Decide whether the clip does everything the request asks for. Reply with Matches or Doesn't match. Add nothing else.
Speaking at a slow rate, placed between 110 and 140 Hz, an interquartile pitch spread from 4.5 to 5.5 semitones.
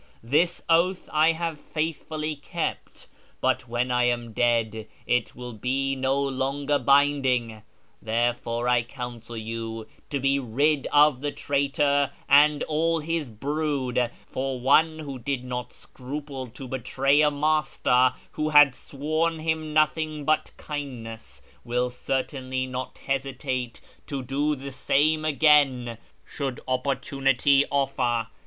Doesn't match